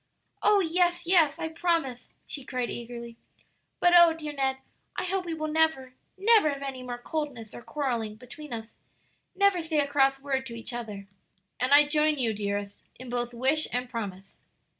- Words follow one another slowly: No, average, 180 wpm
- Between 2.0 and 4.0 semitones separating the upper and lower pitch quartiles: No, average, 4.9 semitones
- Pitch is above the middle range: Yes, very high, 270 Hz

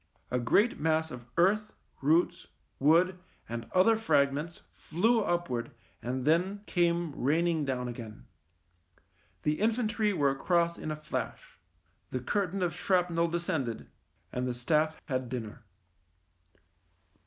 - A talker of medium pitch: Yes, medium, 165 Hz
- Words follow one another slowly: Yes, slow, 130 wpm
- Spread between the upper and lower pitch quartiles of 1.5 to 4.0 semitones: No, wide, 5.4 semitones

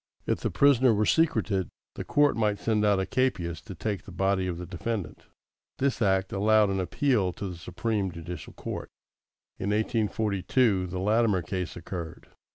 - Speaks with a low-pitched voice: Yes, low, 100 Hz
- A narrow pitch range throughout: No, average, 3.4 semitones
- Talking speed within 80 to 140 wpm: No, average, 165 wpm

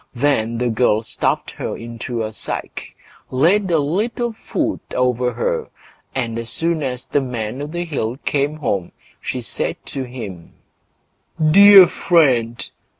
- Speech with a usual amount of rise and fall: No, wide, 5.9 semitones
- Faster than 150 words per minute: No, average, 145 wpm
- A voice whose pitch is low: Yes, low, 130 Hz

